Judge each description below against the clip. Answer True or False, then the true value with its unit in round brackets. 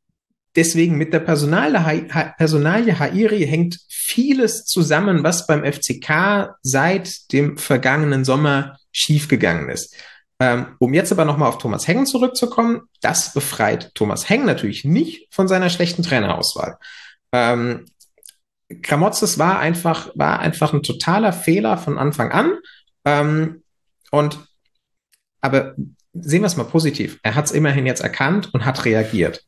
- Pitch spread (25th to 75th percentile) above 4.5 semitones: True (5.2 semitones)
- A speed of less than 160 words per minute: True (130 wpm)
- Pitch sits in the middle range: True (155 Hz)